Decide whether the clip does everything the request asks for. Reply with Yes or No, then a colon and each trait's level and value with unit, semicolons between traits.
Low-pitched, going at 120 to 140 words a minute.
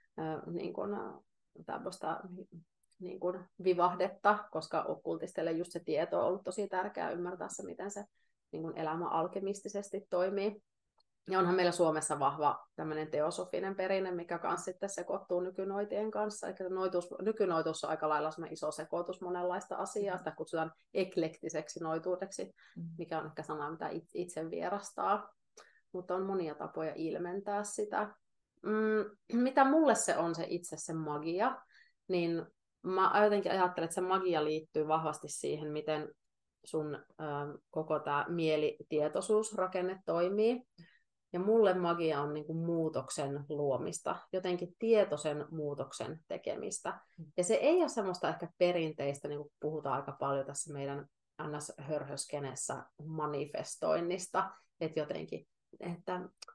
No: medium, 175 Hz; average, 125 wpm